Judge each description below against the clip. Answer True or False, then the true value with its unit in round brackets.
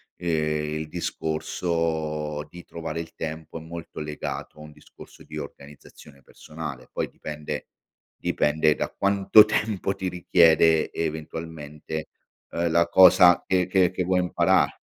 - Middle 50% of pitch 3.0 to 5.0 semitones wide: False (2.4 semitones)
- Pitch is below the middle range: True (80 Hz)